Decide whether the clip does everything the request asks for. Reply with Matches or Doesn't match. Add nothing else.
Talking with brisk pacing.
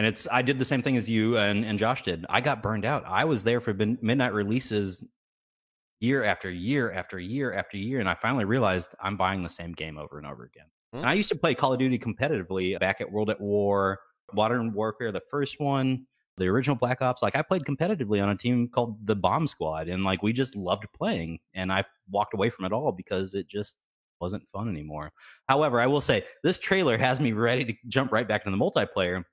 Matches